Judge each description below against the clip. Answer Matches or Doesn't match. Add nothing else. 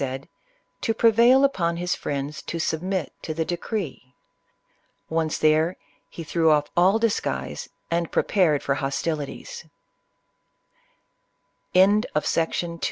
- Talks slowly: Matches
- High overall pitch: Doesn't match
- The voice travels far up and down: Doesn't match